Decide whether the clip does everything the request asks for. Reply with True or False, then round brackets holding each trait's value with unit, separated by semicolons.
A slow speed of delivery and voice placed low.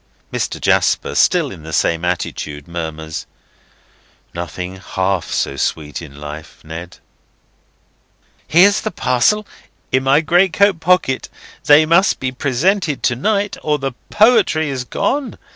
True (125 wpm; 130 Hz)